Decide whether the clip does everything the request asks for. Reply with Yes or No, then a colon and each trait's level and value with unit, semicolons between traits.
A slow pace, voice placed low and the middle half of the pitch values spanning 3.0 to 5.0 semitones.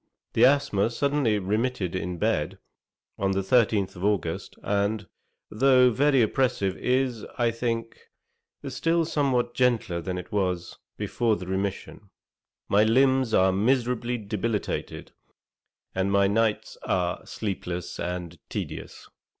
Yes: slow, 125 wpm; low, 110 Hz; average, 4.7 semitones